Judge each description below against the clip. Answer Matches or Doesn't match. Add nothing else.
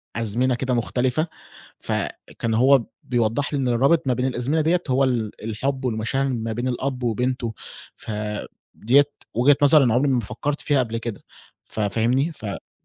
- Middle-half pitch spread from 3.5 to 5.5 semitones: Doesn't match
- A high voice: Doesn't match